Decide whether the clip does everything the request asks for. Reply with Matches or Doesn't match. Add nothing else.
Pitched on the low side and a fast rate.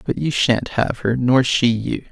Matches